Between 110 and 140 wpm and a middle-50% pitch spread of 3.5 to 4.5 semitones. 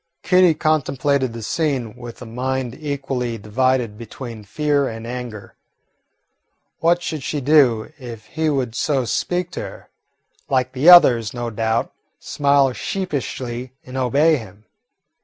Yes: slow, 135 wpm; average, 3.8 semitones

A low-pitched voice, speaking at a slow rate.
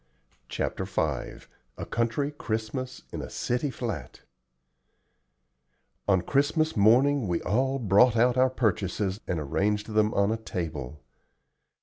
Yes: low, 110 Hz; slow, 120 wpm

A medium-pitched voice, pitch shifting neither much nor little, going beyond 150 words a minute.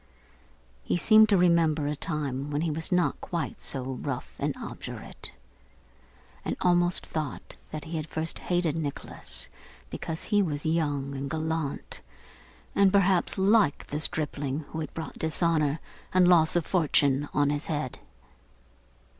No: medium, 160 Hz; average, 3.1 semitones; average, 145 wpm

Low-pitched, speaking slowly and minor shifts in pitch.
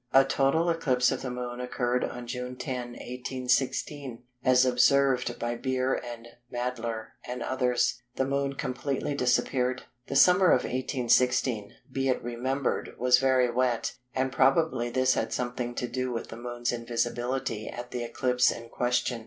No: low, 125 Hz; average, 155 wpm; narrow, 1.4 semitones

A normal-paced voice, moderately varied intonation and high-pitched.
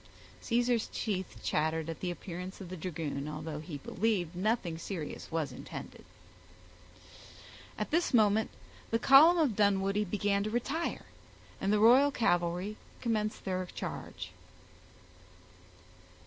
No: slow, 120 wpm; average, 4.8 semitones; high, 195 Hz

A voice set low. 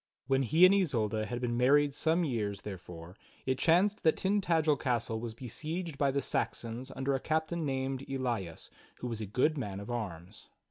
Yes: low, 130 Hz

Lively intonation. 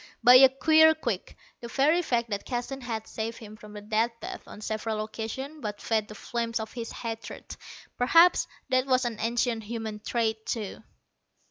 No: average, 2.7 semitones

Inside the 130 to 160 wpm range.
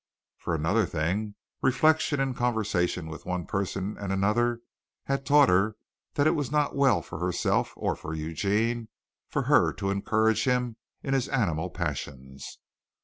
Yes: average, 150 wpm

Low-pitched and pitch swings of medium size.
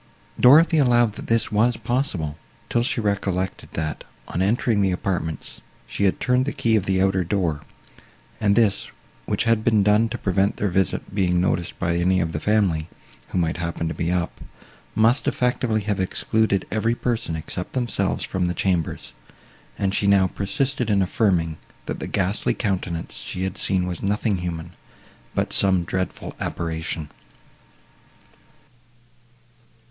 Yes: very low, 95 Hz; average, 3.9 semitones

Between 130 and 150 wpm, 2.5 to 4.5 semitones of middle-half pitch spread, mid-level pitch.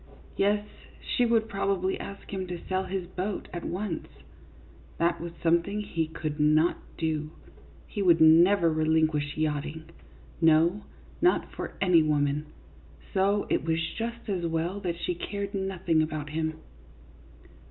Yes: average, 140 wpm; average, 3.7 semitones; medium, 170 Hz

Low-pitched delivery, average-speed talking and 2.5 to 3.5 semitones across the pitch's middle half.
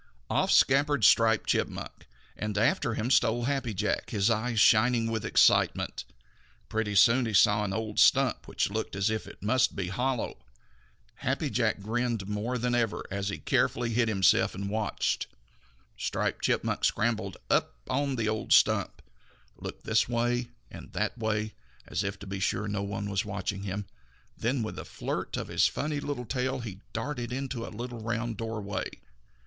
Yes: low, 110 Hz; average, 170 wpm; average, 2.9 semitones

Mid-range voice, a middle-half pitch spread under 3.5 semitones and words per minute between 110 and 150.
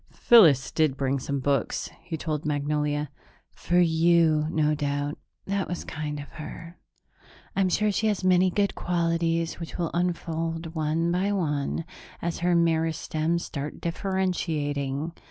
Yes: medium, 165 Hz; average, 2.8 semitones; slow, 135 wpm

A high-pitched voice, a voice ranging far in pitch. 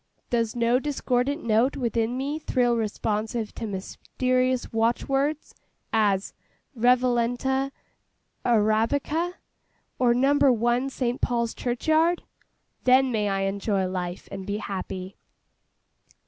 No: high, 240 Hz; average, 3.3 semitones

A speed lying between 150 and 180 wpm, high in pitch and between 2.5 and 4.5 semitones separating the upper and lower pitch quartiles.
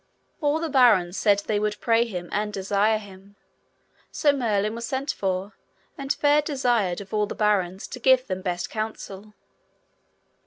Yes: average, 160 wpm; high, 210 Hz; average, 4.2 semitones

